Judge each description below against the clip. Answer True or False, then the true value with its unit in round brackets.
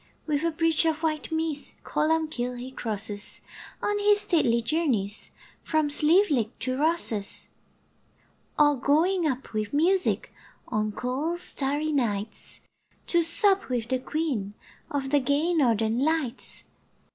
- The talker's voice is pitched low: False (290 Hz)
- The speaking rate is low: True (125 wpm)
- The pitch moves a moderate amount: True (5.0 semitones)